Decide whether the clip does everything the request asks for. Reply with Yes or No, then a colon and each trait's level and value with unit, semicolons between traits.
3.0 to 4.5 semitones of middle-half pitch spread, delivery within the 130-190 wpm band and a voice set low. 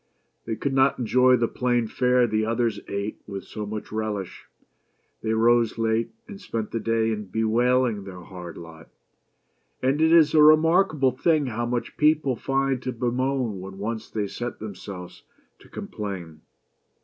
Yes: average, 3.6 semitones; average, 160 wpm; low, 115 Hz